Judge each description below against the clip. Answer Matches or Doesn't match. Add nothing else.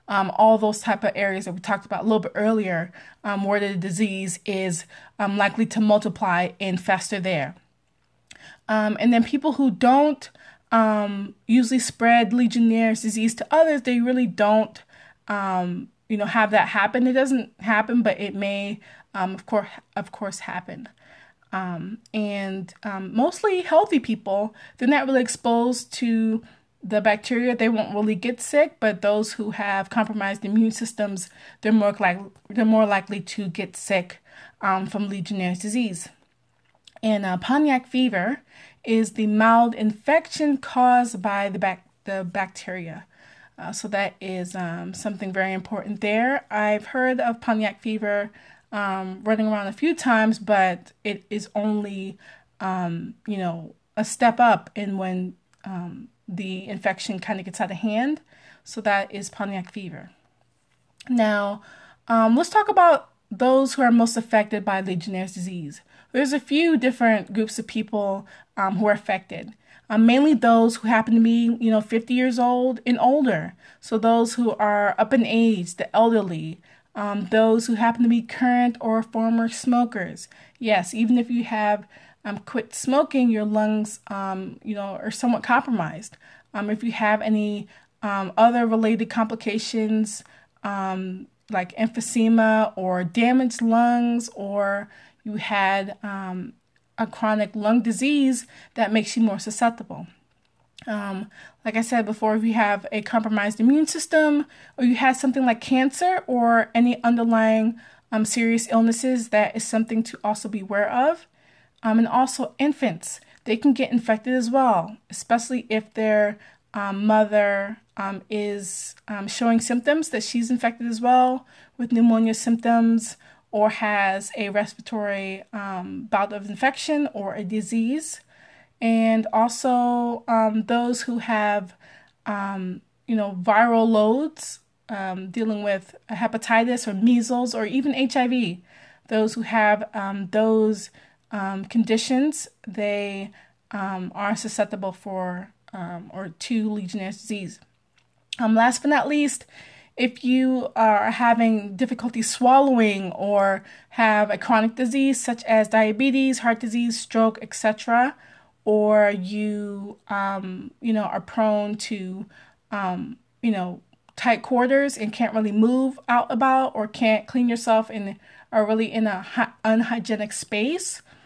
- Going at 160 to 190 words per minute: Doesn't match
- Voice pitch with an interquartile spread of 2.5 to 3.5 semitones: Matches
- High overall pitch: Matches